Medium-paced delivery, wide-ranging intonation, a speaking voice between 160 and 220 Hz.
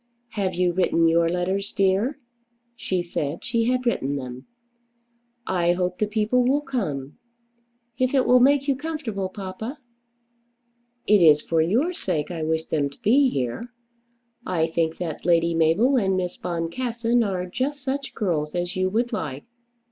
Yes: average, 155 wpm; wide, 6.6 semitones; medium, 185 Hz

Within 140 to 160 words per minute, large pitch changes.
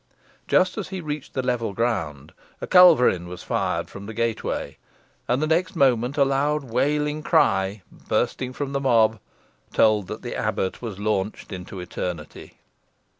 Yes: average, 155 wpm; wide, 6.6 semitones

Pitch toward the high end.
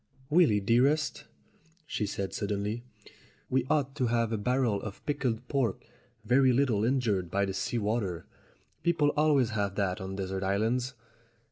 No: low, 115 Hz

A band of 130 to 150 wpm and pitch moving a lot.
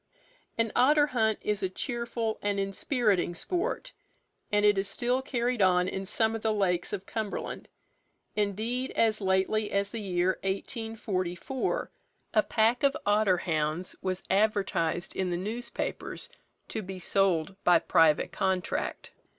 No: average, 140 wpm; average, 3.4 semitones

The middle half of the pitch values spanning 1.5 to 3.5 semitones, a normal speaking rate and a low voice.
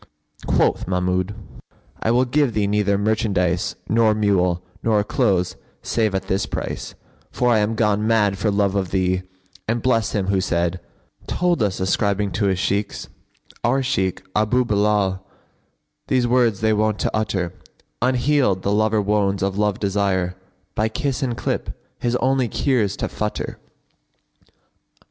Yes: average, 3.0 semitones; average, 155 wpm; low, 105 Hz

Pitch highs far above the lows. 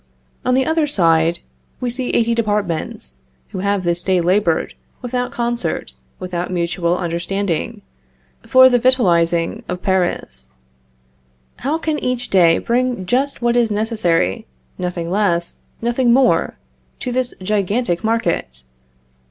Yes: wide, 6.1 semitones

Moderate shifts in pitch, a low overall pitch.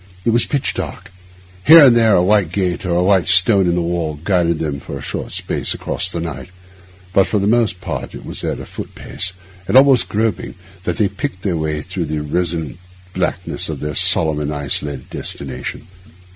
Yes: average, 4.4 semitones; very low, 90 Hz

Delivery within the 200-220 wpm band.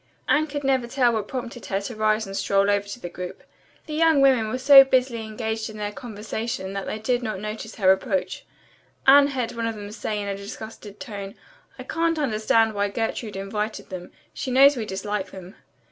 Yes: fast, 205 wpm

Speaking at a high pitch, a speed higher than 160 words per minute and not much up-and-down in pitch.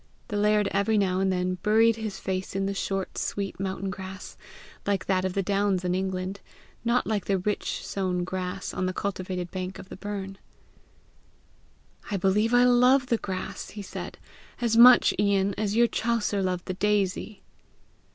Yes: high, 195 Hz; average, 170 wpm; narrow, 2.0 semitones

